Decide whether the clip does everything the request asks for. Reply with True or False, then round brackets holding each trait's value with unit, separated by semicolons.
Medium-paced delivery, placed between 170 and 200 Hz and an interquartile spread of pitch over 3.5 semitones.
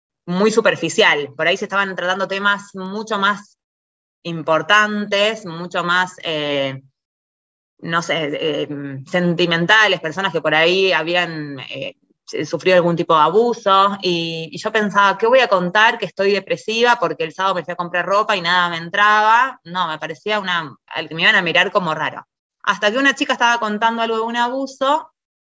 True (175 wpm; 185 Hz; 4.3 semitones)